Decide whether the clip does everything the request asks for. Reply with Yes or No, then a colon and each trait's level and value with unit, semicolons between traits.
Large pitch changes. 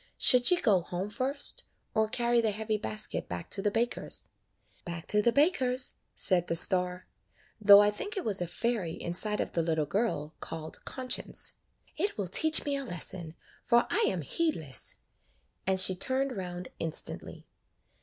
Yes: wide, 5.7 semitones